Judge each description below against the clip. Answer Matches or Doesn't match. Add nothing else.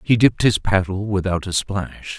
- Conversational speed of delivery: Matches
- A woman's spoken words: Doesn't match